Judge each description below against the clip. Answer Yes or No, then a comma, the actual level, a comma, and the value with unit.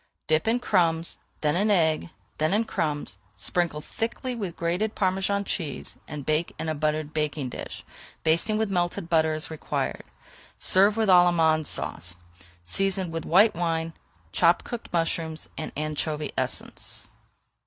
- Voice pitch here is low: No, medium, 165 Hz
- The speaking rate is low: No, average, 145 wpm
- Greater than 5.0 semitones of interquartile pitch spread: No, average, 3.7 semitones